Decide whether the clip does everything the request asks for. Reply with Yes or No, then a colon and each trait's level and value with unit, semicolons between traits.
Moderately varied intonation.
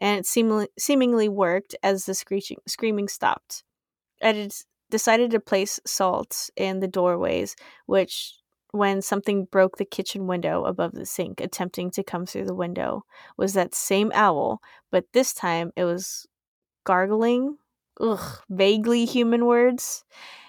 Yes: average, 3.1 semitones